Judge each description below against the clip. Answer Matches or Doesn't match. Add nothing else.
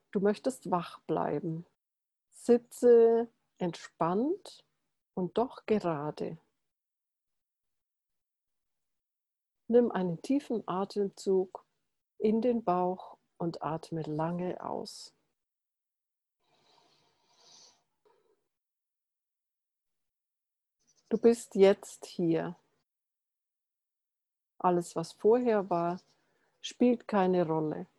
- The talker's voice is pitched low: Doesn't match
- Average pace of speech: Doesn't match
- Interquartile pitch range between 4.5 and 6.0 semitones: Matches